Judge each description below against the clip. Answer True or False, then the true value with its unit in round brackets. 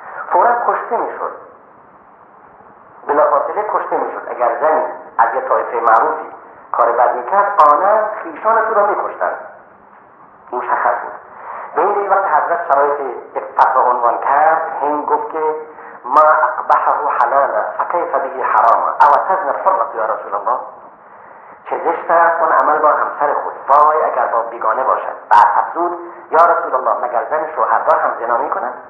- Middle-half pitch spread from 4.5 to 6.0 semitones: True (5.5 semitones)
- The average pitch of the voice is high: False (160 Hz)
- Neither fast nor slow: True (145 wpm)